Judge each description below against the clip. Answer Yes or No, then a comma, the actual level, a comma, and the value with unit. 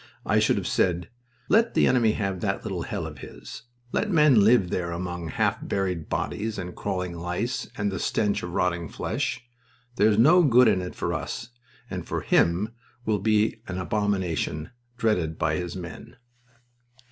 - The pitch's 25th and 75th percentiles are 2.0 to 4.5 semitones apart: Yes, average, 4.0 semitones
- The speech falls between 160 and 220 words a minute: Yes, average, 170 wpm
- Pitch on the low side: Yes, very low, 95 Hz